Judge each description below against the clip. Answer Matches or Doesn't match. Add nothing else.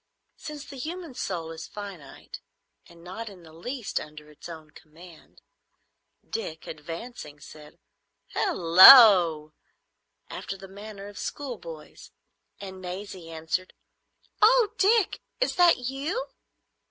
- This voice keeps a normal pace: Doesn't match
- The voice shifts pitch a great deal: Matches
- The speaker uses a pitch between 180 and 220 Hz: Matches